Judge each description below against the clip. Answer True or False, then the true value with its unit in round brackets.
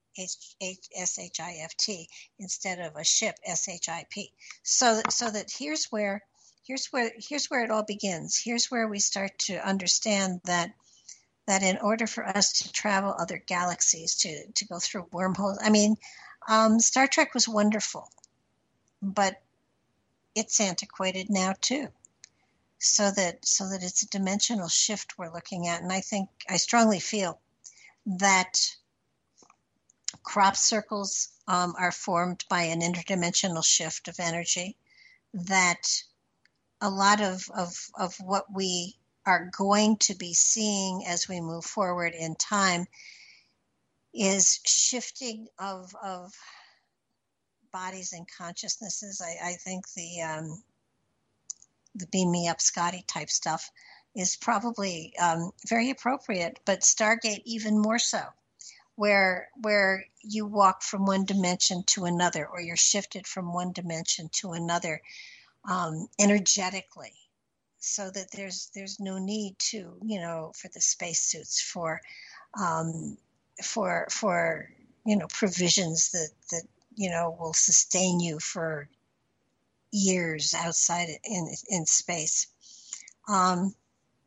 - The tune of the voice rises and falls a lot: False (3.2 semitones)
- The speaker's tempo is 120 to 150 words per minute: True (135 wpm)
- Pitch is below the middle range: False (190 Hz)